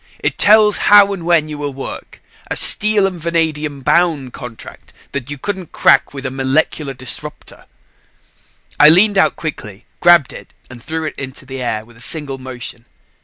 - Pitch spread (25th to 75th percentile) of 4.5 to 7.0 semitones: Yes, average, 4.8 semitones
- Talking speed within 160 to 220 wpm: Yes, average, 170 wpm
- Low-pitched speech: No, medium, 150 Hz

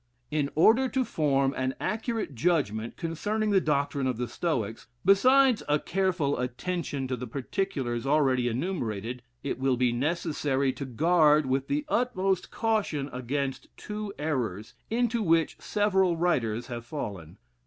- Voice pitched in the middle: Yes, medium, 145 Hz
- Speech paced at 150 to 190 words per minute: No, average, 140 wpm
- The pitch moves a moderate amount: No, wide, 7.1 semitones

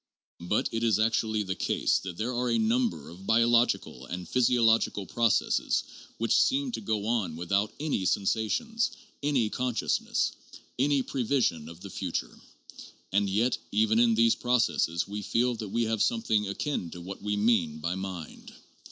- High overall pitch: No, low, 110 Hz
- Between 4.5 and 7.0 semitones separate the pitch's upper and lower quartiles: No, average, 3.8 semitones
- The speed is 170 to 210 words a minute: No, average, 160 wpm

